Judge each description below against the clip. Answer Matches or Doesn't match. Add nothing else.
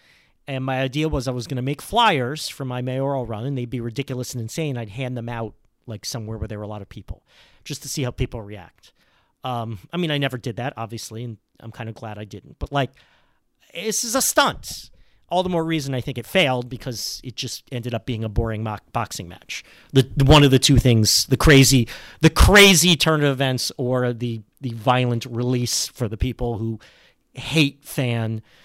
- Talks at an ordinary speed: Doesn't match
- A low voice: Matches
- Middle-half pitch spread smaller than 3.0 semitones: Doesn't match